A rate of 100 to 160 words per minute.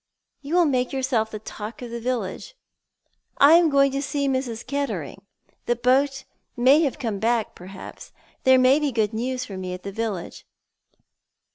No: average, 170 wpm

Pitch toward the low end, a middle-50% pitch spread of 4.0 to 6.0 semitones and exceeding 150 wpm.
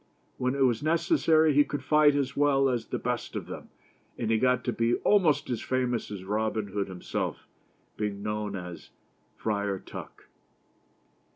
Yes: low, 120 Hz; average, 5.3 semitones; average, 170 wpm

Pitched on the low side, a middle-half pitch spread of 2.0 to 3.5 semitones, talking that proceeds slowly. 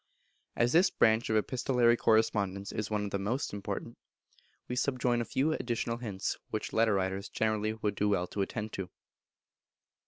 No: low, 110 Hz; average, 2.9 semitones; average, 165 wpm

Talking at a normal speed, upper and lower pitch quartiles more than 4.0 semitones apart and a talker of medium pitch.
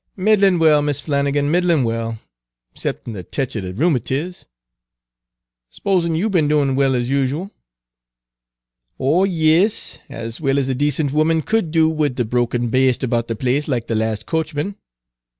Yes: average, 165 wpm; average, 4.7 semitones; medium, 145 Hz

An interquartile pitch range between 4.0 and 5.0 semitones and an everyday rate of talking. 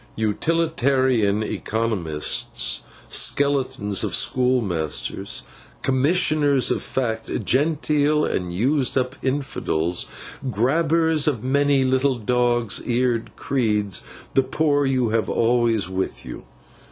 No: average, 4.6 semitones; slow, 100 wpm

